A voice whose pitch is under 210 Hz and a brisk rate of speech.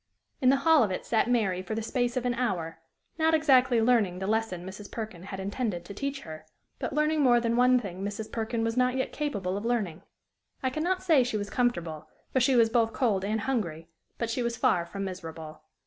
No: high, 225 Hz; fast, 225 wpm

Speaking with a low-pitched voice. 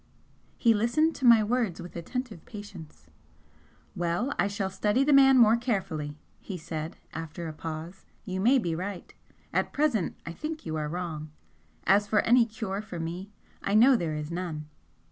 No: high, 195 Hz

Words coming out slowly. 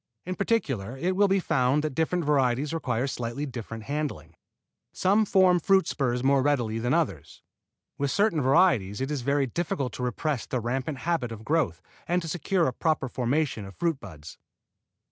No: average, 175 wpm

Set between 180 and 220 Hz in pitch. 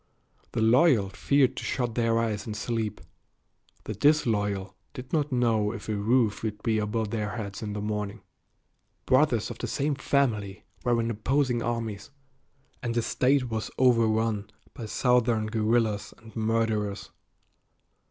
No: low, 115 Hz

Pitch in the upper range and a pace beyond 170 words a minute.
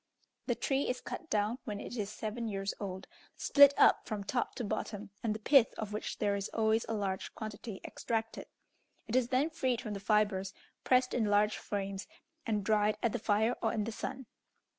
Yes: high, 215 Hz; average, 200 wpm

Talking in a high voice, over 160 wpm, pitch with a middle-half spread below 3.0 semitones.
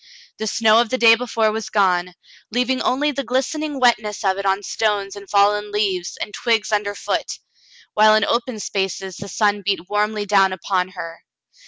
Yes: high, 210 Hz; average, 180 wpm; narrow, 2.6 semitones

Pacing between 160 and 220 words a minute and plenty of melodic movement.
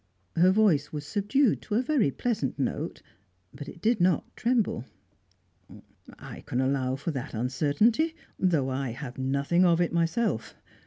No: average, 150 wpm; wide, 7.9 semitones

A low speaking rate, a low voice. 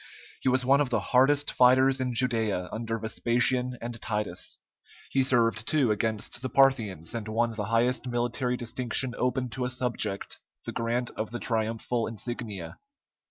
No: average, 160 wpm; low, 120 Hz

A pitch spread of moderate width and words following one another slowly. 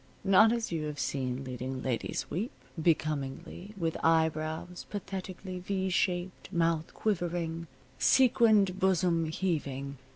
Yes: average, 3.6 semitones; slow, 110 wpm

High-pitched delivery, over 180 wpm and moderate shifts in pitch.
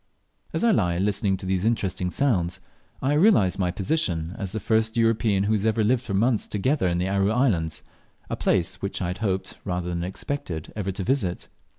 No: low, 100 Hz; average, 200 wpm; average, 3.9 semitones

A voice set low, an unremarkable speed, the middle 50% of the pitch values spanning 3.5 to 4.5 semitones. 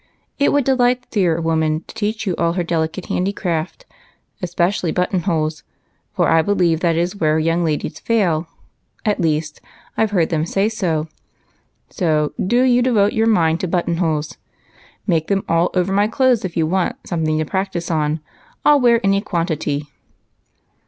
No: medium, 175 Hz; average, 170 wpm; average, 4.1 semitones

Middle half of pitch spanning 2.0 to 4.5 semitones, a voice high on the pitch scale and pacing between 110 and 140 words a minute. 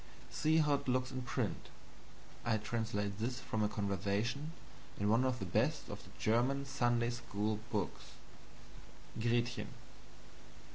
No: average, 3.5 semitones; low, 120 Hz; slow, 135 wpm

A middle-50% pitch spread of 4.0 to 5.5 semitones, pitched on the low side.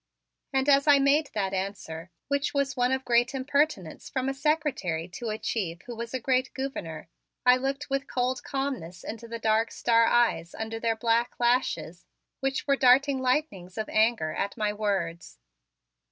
No: average, 4.7 semitones; high, 240 Hz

